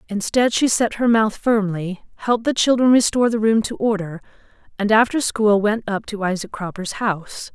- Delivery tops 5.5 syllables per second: No, 5.1 syllables/s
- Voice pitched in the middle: No, high, 215 Hz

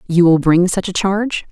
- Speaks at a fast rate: Yes, fast, 235 wpm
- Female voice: Yes, female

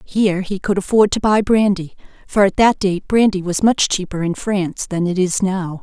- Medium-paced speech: No, fast, 215 wpm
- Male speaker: No, female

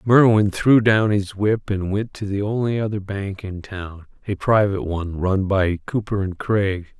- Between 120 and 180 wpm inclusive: No, average, 190 wpm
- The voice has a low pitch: Yes, low, 100 Hz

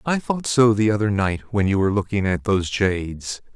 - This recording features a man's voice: Yes, male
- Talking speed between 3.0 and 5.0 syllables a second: No, 5.4 syllables/s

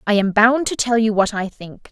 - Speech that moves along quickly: Yes, fast, 280 wpm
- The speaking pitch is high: Yes, high, 220 Hz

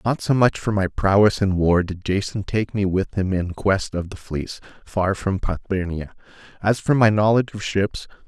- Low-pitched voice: Yes, low, 100 Hz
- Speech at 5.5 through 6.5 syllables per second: No, 4.9 syllables/s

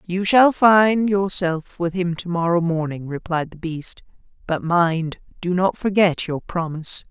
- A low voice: No, medium, 175 Hz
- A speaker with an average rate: Yes, average, 160 wpm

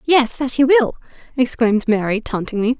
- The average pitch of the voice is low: No, high, 245 Hz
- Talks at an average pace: Yes, average, 150 wpm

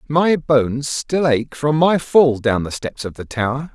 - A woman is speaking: No, male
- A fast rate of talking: Yes, fast, 210 wpm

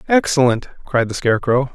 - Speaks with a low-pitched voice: Yes, low, 130 Hz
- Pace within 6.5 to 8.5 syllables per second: No, 5.7 syllables/s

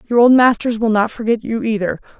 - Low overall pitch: No, high, 220 Hz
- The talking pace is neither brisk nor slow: No, fast, 220 wpm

